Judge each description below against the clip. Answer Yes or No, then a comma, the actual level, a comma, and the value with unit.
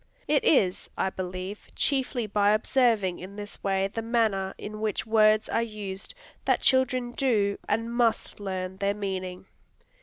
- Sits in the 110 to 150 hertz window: No, high, 210 Hz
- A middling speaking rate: Yes, average, 150 wpm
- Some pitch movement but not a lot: Yes, average, 3.1 semitones